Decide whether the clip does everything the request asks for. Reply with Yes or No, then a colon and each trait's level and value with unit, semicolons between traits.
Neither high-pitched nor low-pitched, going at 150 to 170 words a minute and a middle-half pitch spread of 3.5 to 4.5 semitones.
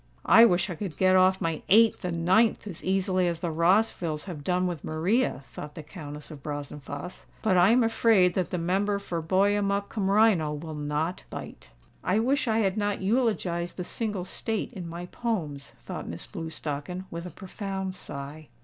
No: medium, 180 Hz; average, 185 wpm; average, 4.0 semitones